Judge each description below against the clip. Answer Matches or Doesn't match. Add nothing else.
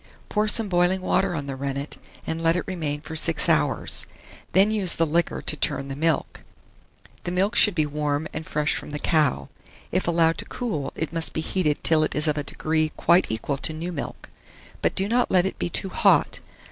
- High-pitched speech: Doesn't match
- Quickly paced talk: Matches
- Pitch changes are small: Doesn't match